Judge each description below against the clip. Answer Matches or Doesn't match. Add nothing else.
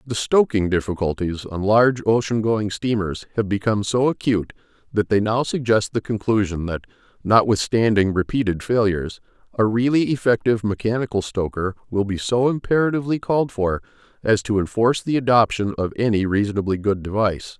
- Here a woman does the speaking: Doesn't match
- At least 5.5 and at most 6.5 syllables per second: Matches